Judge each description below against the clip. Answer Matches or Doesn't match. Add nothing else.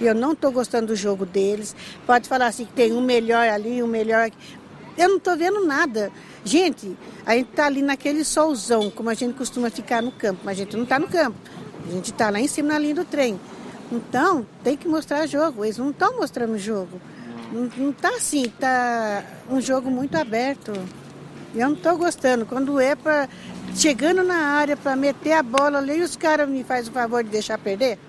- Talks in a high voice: Matches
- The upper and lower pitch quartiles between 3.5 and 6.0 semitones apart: Matches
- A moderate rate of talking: Doesn't match